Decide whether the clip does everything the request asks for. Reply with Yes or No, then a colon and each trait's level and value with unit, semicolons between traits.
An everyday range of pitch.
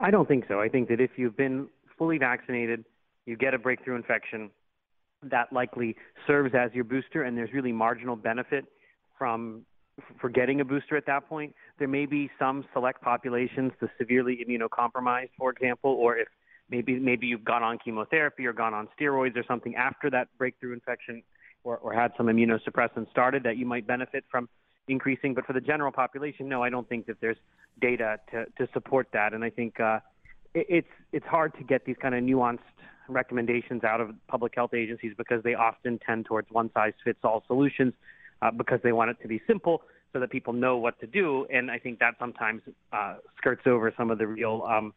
No: narrow, 2.2 semitones